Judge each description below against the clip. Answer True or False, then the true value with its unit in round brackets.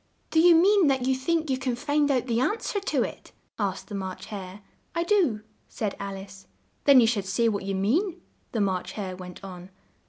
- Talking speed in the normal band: False (215 wpm)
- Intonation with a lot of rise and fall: True (7.4 semitones)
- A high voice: True (230 Hz)